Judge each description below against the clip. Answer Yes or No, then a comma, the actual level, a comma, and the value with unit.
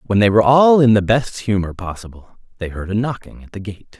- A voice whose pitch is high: No, low, 105 Hz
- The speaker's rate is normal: No, fast, 240 wpm